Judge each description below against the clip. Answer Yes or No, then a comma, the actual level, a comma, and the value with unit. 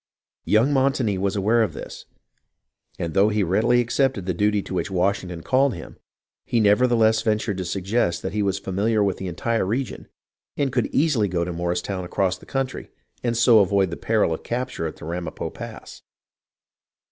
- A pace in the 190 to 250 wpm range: No, average, 180 wpm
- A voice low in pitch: Yes, low, 105 Hz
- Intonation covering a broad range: No, average, 4.2 semitones